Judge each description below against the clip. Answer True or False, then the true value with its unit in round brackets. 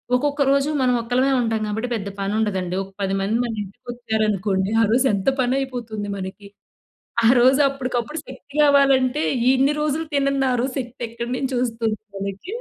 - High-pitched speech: True (240 Hz)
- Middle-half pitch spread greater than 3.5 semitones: True (4.3 semitones)